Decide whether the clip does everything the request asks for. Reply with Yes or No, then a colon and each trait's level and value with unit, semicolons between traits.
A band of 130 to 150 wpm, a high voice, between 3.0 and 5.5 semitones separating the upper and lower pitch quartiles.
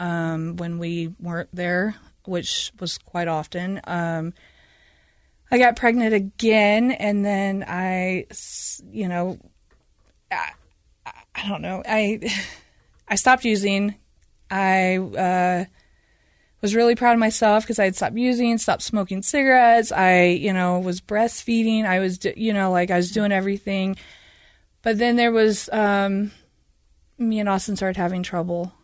Yes: average, 140 wpm; high, 195 Hz; average, 3.5 semitones